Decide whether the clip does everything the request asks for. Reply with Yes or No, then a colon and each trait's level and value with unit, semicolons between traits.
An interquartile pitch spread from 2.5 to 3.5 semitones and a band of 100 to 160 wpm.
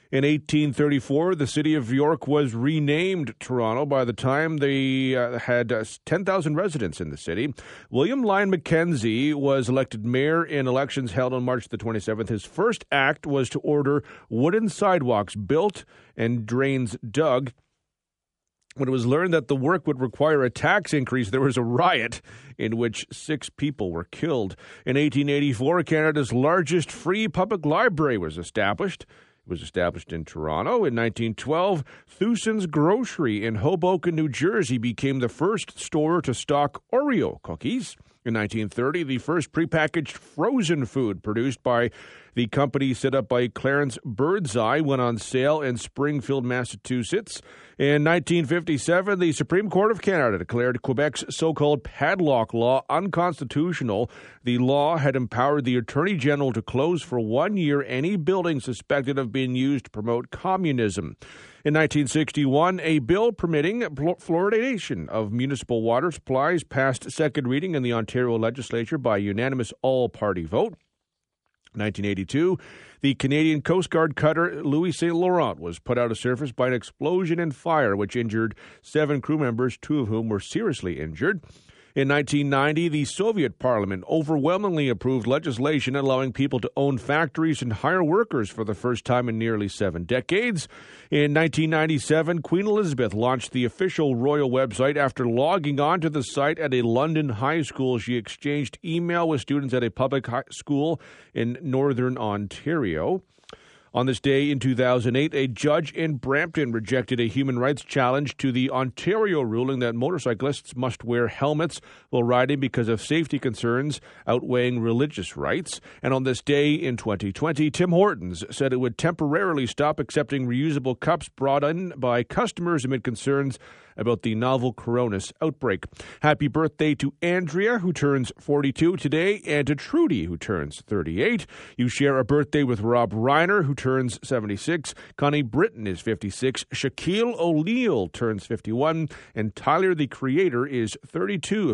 No: average, 4.2 semitones; average, 150 wpm